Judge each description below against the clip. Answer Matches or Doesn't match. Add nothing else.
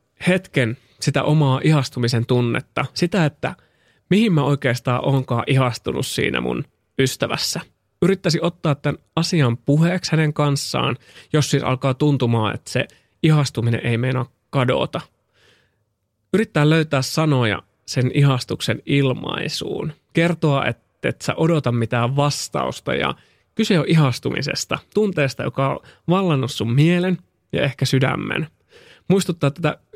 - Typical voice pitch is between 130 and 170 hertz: Matches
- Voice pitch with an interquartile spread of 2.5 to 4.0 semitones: Doesn't match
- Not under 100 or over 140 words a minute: Matches